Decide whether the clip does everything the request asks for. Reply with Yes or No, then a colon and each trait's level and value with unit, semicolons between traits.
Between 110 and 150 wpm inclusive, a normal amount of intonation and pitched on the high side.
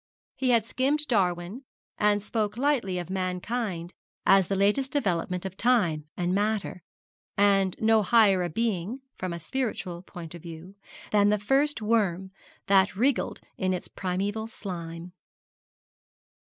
Yes: average, 140 wpm; average, 3.9 semitones; high, 195 Hz